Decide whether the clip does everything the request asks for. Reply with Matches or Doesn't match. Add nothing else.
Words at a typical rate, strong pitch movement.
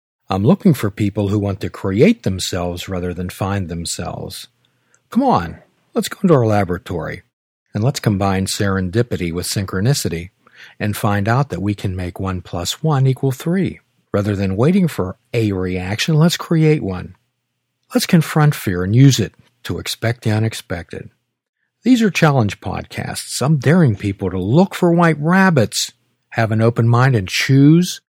Matches